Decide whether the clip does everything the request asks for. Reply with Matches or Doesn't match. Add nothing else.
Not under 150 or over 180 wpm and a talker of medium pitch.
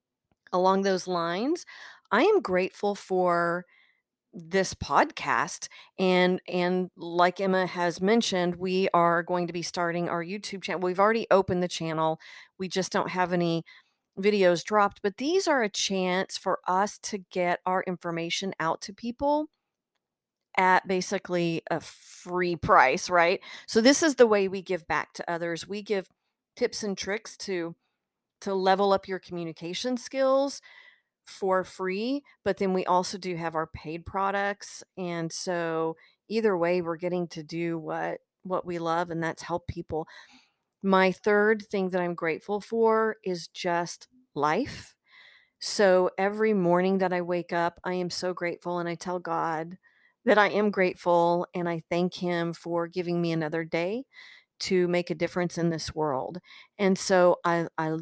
Matches